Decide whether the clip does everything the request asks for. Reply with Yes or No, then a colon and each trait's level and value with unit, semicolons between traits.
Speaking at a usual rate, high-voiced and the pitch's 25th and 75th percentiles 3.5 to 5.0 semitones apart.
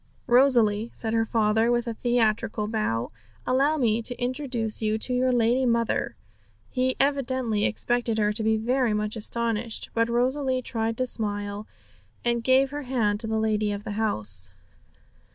No: average, 160 wpm; high, 230 Hz; narrow, 2.6 semitones